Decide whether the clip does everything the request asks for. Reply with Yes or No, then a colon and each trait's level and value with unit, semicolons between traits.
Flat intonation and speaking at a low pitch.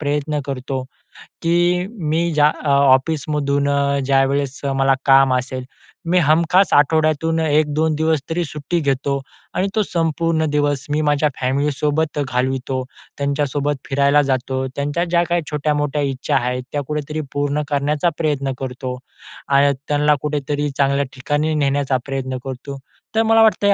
No: narrow, 2.2 semitones; medium, 145 Hz